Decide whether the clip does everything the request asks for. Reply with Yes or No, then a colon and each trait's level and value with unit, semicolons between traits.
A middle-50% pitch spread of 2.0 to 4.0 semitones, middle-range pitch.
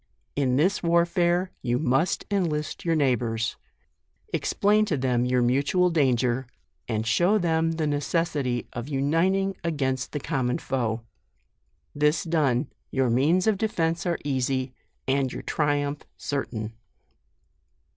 No: average, 4.9 semitones; medium, 145 Hz